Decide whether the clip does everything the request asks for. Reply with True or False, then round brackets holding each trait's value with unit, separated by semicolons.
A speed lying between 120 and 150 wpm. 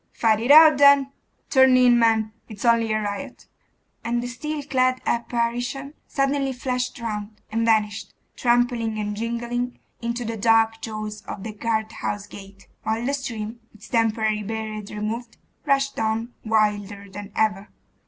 True (145 wpm)